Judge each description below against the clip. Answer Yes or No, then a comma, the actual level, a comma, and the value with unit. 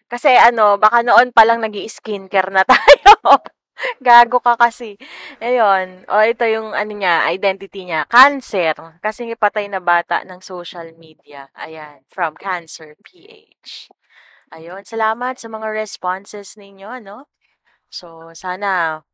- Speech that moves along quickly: No, average, 130 wpm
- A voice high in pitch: Yes, high, 205 Hz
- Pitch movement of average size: Yes, average, 4.5 semitones